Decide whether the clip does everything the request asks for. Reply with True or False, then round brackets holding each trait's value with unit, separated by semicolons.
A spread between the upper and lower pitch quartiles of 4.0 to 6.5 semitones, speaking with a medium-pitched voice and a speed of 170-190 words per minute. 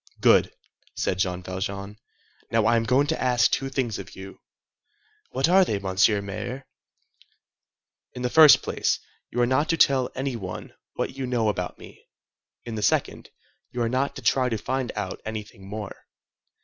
False (4.7 semitones; 115 Hz; 175 wpm)